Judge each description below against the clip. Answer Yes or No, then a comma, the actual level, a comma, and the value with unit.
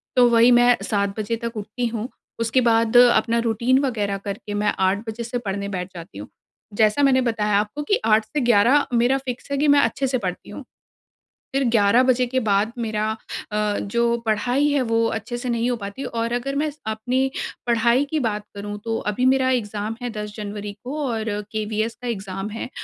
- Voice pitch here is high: Yes, high, 230 Hz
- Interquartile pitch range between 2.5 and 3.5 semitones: Yes, average, 2.9 semitones